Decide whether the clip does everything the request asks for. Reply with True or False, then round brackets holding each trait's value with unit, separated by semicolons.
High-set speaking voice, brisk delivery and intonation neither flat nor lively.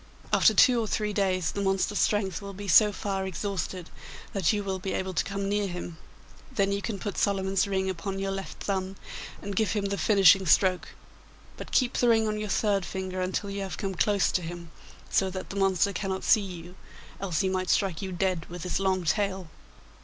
False (195 Hz; 210 wpm; 1.4 semitones)